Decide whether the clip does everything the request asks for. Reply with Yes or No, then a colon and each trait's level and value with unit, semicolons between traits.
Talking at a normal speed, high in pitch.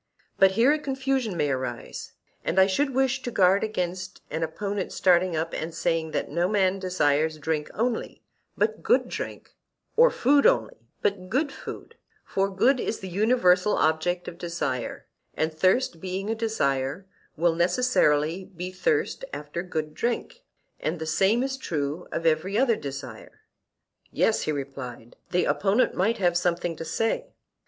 No: average, 160 wpm; medium, 180 Hz